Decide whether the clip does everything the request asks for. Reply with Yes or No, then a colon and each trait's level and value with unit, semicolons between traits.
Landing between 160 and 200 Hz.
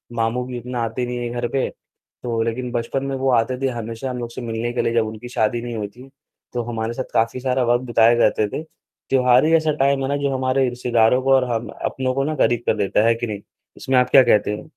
No: low, 120 Hz